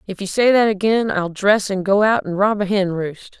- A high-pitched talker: Yes, high, 200 Hz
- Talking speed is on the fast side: Yes, fast, 265 wpm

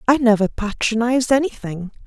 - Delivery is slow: Yes, slow, 115 wpm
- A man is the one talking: No, female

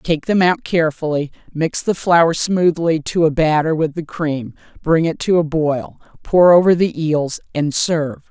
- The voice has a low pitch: No, medium, 160 Hz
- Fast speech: No, average, 180 wpm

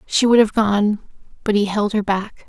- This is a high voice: Yes, high, 210 Hz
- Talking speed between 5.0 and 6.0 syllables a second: No, 4.6 syllables/s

